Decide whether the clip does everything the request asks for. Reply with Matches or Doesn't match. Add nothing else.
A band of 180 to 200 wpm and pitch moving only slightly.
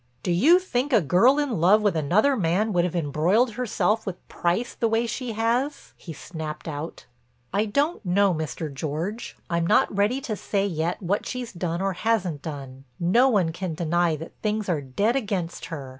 Doesn't match